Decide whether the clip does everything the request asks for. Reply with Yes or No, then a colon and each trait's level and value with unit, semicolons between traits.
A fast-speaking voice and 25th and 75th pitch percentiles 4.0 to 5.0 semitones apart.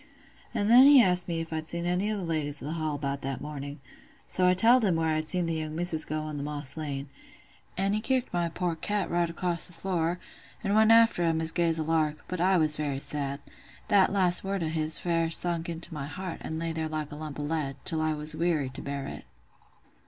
No: fast, 245 wpm; average, 2.8 semitones